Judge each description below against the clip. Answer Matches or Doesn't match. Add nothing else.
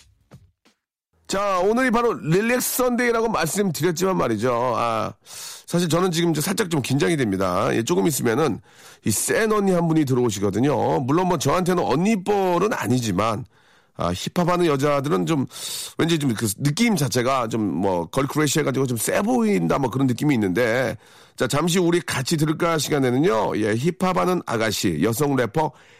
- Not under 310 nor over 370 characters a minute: Matches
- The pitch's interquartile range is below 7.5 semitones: Matches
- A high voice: Doesn't match